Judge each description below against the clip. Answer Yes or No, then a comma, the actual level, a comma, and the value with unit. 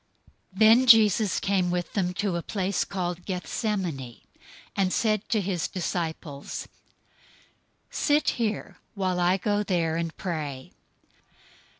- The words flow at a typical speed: No, slow, 120 wpm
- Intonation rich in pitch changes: No, average, 3.4 semitones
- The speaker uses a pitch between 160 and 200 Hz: Yes, medium, 185 Hz